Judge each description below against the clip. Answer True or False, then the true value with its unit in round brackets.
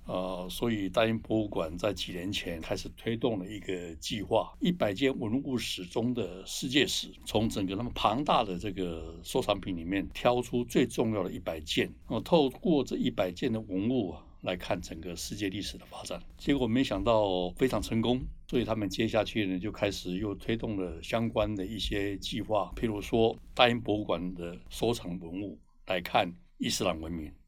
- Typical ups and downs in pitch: True (3.9 semitones)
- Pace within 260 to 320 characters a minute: True (285 characters per minute)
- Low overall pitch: True (100 Hz)